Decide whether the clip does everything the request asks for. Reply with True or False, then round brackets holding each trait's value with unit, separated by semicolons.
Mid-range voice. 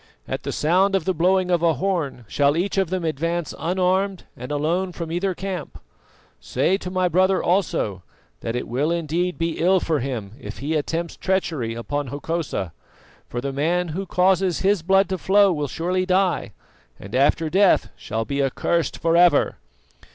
True (170 Hz)